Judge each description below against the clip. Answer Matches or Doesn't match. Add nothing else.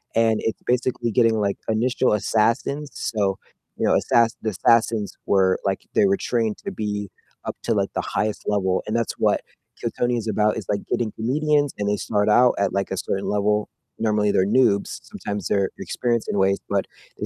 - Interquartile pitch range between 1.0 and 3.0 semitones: Matches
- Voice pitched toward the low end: Matches